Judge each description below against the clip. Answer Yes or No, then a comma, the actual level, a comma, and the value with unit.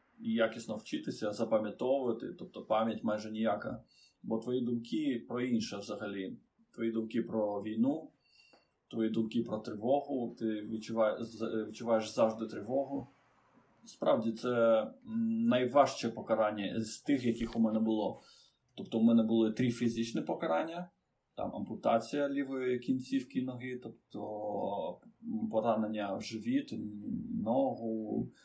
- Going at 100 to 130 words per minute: Yes, average, 110 wpm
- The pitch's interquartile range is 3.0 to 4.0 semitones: Yes, average, 3.5 semitones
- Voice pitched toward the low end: Yes, low, 115 Hz